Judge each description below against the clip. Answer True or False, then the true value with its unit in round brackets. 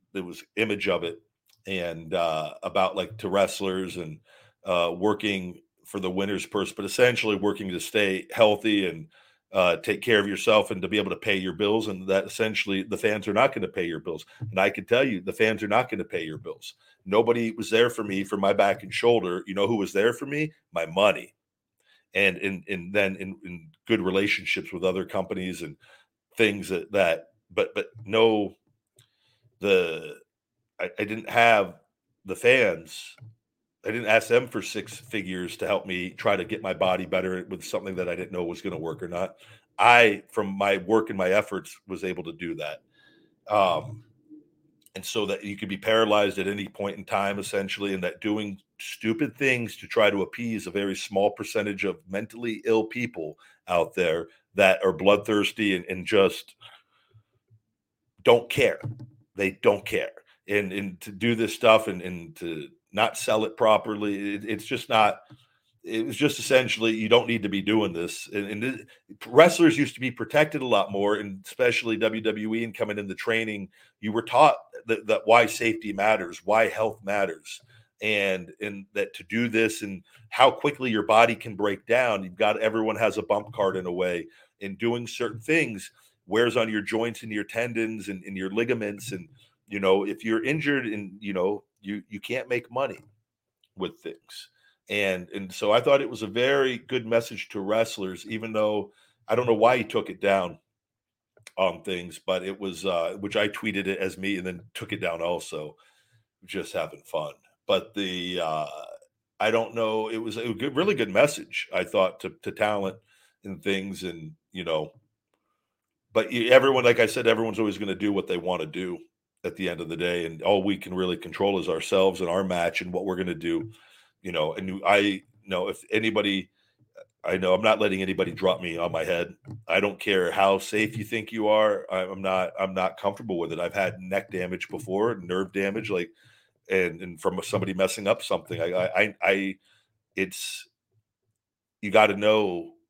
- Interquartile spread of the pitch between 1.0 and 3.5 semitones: True (2.9 semitones)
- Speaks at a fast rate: False (195 wpm)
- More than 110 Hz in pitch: False (105 Hz)